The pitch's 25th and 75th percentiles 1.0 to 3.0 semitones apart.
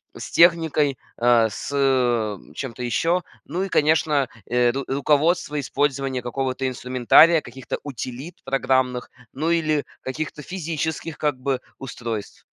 No: average, 3.6 semitones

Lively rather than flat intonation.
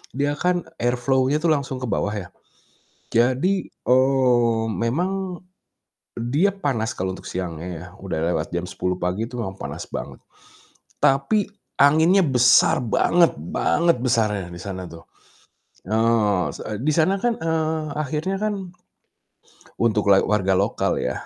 Yes: wide, 7.3 semitones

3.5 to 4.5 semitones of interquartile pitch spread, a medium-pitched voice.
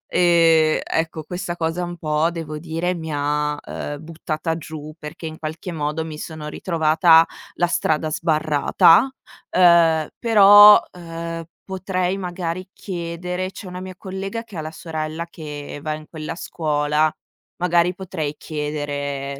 No: narrow, 2.5 semitones; medium, 165 Hz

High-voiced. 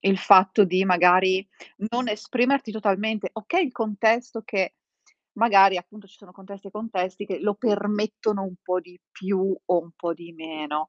Yes: high, 195 Hz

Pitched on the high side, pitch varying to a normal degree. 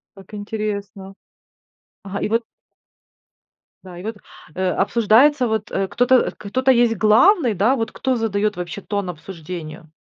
Yes: high, 210 Hz; average, 3.5 semitones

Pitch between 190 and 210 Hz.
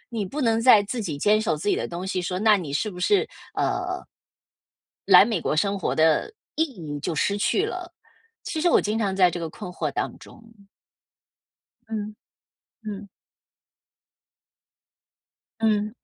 Yes: high, 205 Hz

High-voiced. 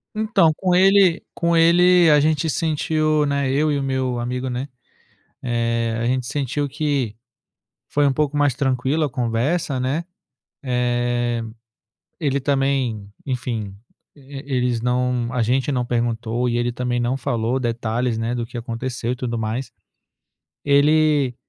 No: low, 130 Hz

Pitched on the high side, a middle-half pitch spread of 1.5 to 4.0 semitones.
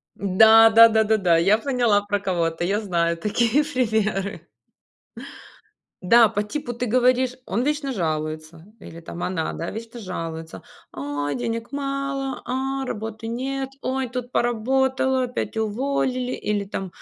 No: high, 225 Hz; average, 5.1 semitones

